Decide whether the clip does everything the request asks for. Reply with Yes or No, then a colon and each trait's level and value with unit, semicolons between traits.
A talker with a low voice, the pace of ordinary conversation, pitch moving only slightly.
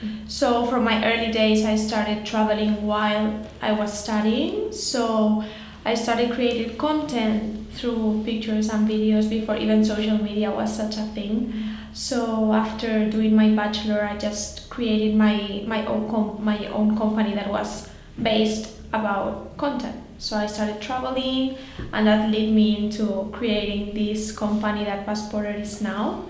No: high, 215 Hz; average, 150 wpm; narrow, 0.9 semitones